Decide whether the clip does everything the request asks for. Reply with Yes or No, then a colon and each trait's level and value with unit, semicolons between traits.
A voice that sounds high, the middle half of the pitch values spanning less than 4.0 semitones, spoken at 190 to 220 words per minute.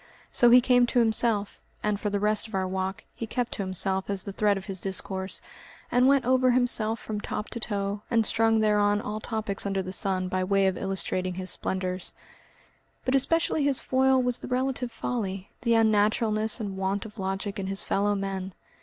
Yes: high, 210 Hz; average, 3.4 semitones; average, 200 wpm